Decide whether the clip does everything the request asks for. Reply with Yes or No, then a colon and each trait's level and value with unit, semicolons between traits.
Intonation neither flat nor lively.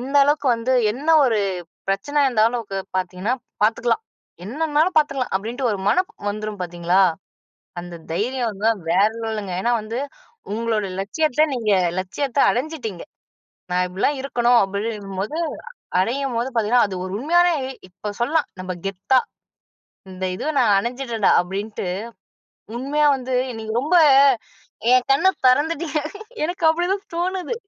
No: wide, 5.9 semitones